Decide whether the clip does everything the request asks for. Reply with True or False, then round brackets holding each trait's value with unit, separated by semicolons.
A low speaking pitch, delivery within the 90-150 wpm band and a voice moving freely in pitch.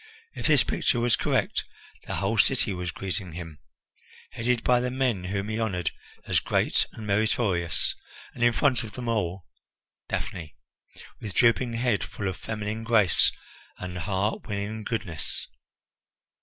False (105 Hz; 145 wpm; 4.2 semitones)